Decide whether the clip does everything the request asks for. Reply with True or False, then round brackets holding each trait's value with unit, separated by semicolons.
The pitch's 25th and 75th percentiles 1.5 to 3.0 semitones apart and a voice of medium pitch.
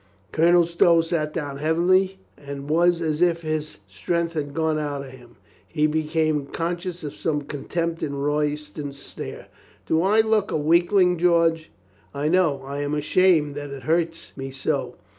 True (2.7 semitones; 155 Hz)